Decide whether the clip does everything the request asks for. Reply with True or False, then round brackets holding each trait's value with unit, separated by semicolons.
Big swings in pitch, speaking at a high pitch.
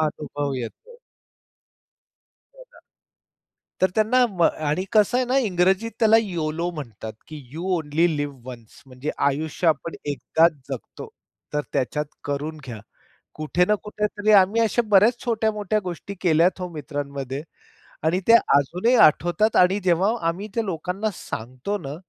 False (6.0 semitones; 170 Hz)